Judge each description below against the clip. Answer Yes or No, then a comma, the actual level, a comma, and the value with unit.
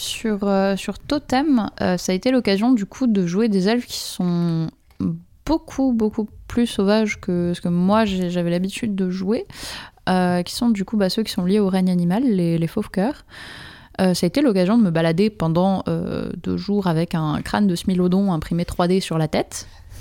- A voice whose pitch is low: No, high, 190 Hz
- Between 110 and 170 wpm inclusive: No, average, 200 wpm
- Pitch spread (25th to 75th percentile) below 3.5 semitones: No, average, 3.8 semitones